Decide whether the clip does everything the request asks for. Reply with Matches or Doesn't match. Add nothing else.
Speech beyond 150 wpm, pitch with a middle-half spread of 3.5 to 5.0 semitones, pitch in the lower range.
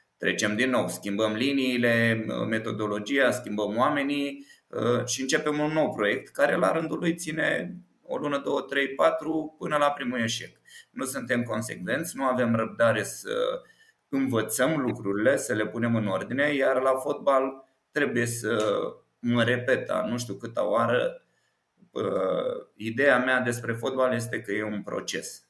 Doesn't match